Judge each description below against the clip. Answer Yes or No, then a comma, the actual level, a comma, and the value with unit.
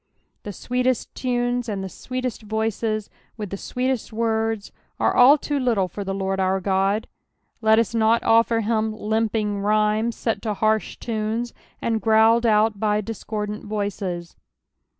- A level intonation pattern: Yes, narrow, 1.8 semitones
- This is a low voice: No, high, 220 Hz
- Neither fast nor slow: Yes, average, 145 wpm